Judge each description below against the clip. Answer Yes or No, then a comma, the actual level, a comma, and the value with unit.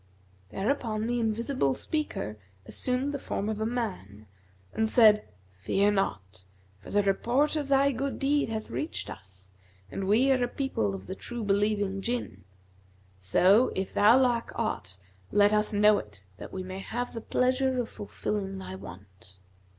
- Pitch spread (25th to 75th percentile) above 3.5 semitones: Yes, average, 4.8 semitones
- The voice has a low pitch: No, high, 210 Hz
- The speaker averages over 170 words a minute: No, average, 160 wpm